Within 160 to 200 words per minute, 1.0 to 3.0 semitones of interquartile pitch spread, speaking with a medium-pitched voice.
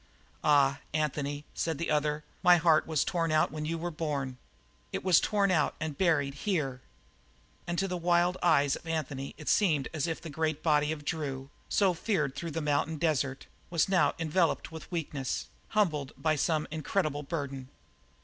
Yes: average, 175 wpm; average, 2.7 semitones; medium, 155 Hz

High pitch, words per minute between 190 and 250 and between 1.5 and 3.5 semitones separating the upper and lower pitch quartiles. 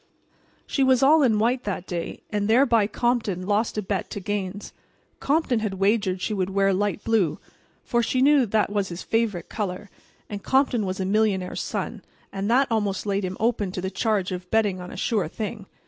Yes: high, 205 Hz; average, 195 wpm; average, 3.2 semitones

